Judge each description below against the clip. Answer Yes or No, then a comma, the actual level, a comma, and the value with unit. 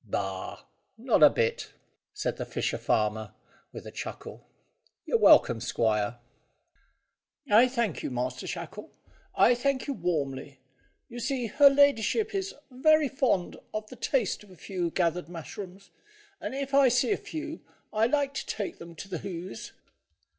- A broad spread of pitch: Yes, wide, 8.5 semitones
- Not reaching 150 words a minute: No, average, 155 wpm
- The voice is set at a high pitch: Yes, high, 210 Hz